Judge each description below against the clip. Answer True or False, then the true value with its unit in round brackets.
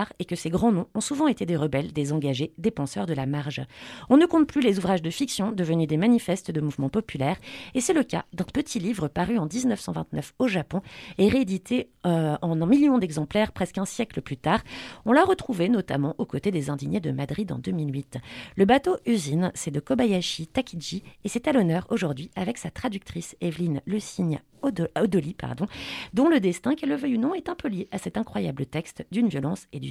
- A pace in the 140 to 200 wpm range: False (215 wpm)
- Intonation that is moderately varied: False (6.8 semitones)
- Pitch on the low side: False (190 Hz)